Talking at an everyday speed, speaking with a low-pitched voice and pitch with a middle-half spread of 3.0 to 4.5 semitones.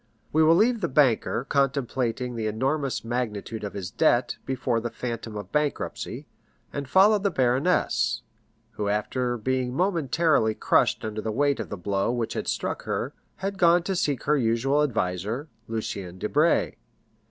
No: average, 155 wpm; low, 125 Hz; average, 5.1 semitones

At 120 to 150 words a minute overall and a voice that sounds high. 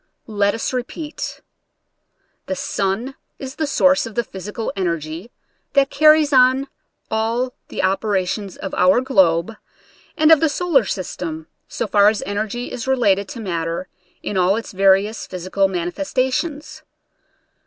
Yes: average, 140 wpm; high, 215 Hz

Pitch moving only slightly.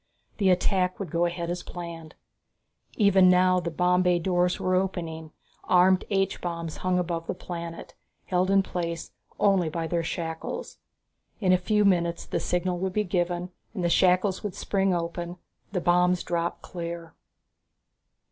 Yes: narrow, 1.5 semitones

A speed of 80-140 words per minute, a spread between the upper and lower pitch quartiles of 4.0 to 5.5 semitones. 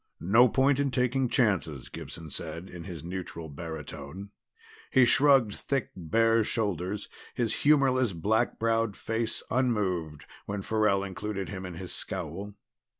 Yes: slow, 135 wpm; average, 5.0 semitones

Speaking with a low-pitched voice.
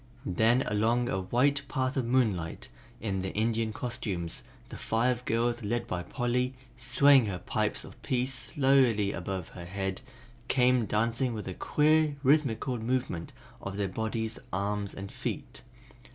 Yes: low, 115 Hz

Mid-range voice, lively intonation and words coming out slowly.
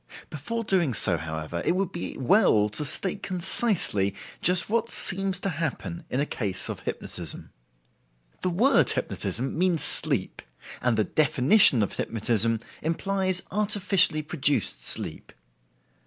Yes: medium, 165 Hz; wide, 8.6 semitones; slow, 130 wpm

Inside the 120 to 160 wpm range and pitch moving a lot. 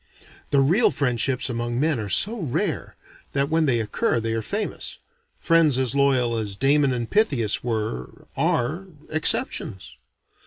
No: average, 145 wpm; average, 4.8 semitones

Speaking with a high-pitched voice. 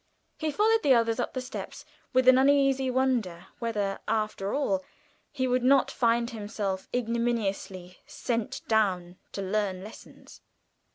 Yes: high, 230 Hz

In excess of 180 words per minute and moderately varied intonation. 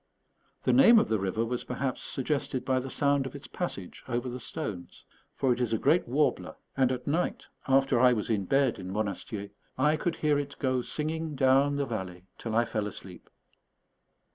Yes: average, 190 wpm; average, 4.3 semitones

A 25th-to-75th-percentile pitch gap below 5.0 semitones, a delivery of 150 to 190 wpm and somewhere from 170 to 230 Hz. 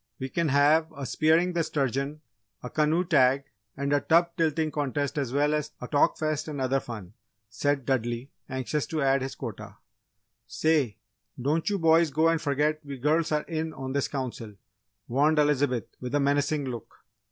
No: average, 2.9 semitones; average, 175 wpm; medium, 145 Hz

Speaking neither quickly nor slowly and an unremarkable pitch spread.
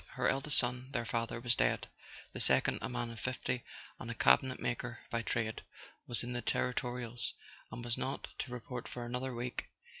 No: average, 180 wpm; narrow, 1.1 semitones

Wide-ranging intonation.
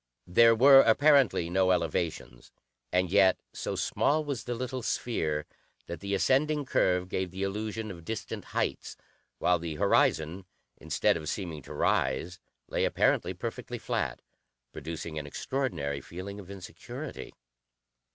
Yes: wide, 5.7 semitones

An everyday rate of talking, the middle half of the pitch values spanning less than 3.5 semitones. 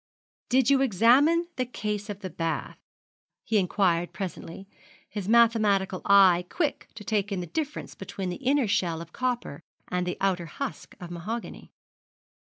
No: average, 155 wpm; average, 5.0 semitones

